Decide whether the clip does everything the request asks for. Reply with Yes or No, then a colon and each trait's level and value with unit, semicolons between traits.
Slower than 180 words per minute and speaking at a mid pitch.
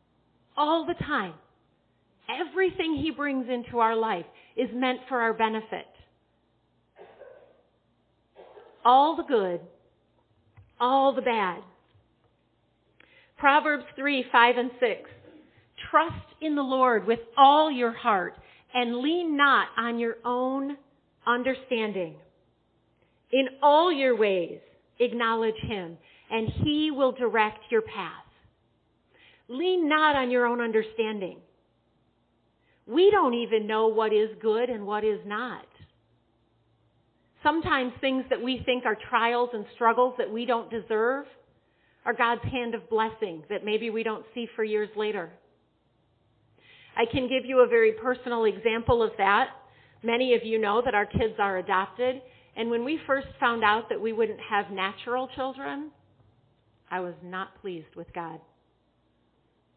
No: slow, 135 wpm; high, 235 Hz